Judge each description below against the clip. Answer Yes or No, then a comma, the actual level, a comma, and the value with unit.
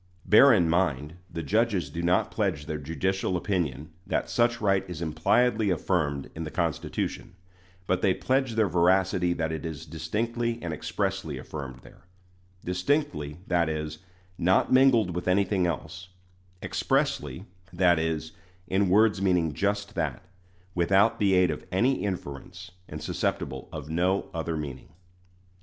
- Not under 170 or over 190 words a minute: No, average, 145 wpm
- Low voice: Yes, very low, 90 Hz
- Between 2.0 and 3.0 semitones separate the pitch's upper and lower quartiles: No, average, 3.8 semitones